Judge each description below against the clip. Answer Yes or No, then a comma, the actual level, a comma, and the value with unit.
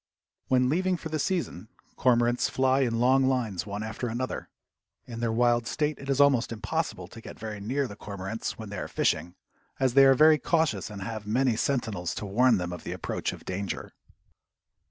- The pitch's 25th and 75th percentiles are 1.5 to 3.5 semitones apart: No, average, 4.2 semitones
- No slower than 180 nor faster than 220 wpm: Yes, average, 195 wpm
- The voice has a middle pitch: No, low, 120 Hz